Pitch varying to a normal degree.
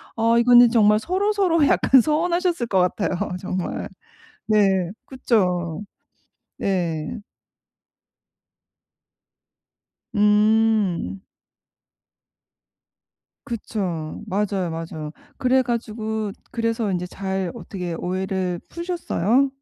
Yes: average, 4.8 semitones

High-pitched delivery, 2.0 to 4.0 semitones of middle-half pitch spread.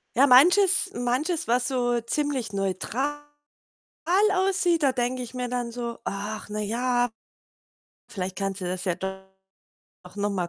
No: high, 245 Hz; average, 5.2 semitones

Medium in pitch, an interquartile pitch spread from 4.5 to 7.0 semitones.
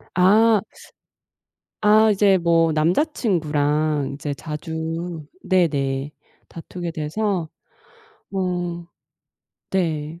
No: medium, 170 Hz; average, 3.6 semitones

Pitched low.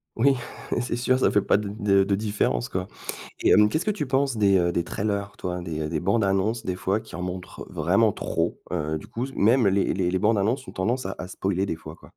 Yes: low, 100 Hz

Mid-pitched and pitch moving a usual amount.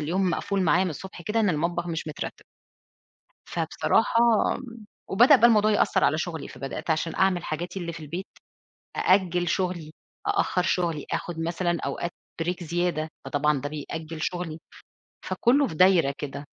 Yes: medium, 175 Hz; average, 3.1 semitones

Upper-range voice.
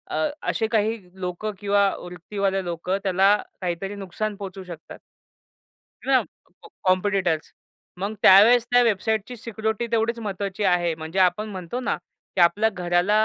Yes: high, 195 Hz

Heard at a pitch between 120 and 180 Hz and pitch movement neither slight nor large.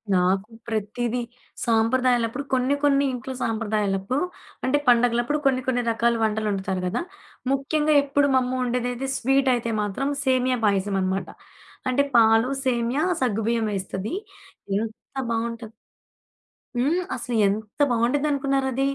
No: high, 240 Hz; average, 3.1 semitones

